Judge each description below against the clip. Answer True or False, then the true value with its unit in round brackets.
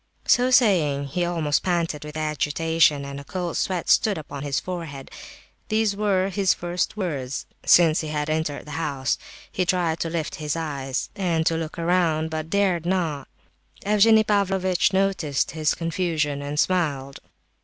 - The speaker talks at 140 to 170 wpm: True (155 wpm)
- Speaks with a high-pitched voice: False (165 Hz)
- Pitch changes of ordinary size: True (3.7 semitones)